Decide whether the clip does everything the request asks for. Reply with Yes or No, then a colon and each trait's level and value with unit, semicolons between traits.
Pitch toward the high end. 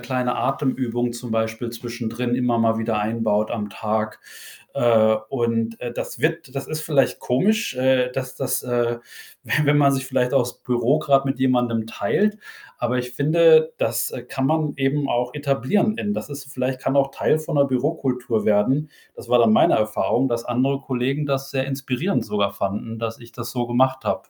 No: low, 125 Hz